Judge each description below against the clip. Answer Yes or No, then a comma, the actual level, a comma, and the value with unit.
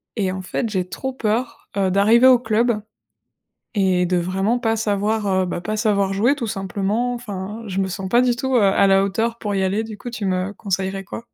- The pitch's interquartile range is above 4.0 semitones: No, average, 3.2 semitones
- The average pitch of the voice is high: Yes, high, 205 Hz